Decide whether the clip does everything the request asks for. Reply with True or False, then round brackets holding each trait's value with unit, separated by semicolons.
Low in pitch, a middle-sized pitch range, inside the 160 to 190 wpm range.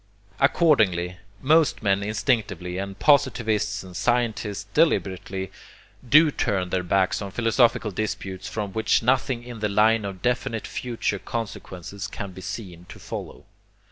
False (105 Hz; 4.0 semitones; 135 wpm)